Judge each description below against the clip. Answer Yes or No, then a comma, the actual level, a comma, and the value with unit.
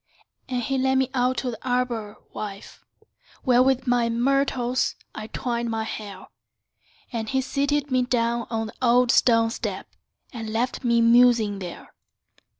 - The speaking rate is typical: Yes, average, 150 wpm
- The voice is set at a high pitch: Yes, high, 240 Hz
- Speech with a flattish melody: Yes, narrow, 2.1 semitones